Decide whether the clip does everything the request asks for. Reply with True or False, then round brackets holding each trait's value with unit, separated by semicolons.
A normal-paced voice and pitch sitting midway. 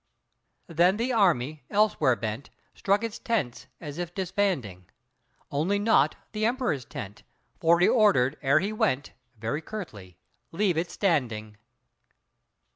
False (125 wpm; 165 Hz)